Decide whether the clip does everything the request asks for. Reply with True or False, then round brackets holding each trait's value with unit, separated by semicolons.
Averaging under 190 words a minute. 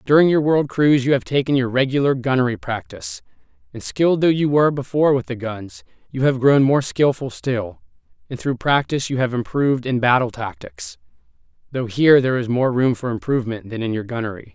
False (195 wpm)